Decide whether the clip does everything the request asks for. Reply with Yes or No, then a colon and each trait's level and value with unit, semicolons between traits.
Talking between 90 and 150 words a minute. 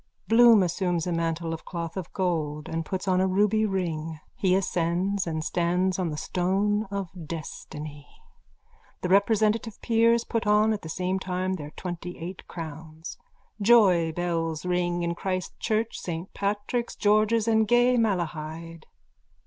Yes: average, 140 wpm